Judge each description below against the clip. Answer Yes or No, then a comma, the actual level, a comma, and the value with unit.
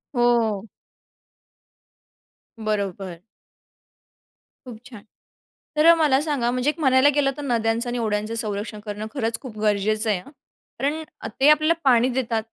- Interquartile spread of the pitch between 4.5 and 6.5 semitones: No, average, 3.9 semitones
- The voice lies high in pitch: Yes, high, 235 Hz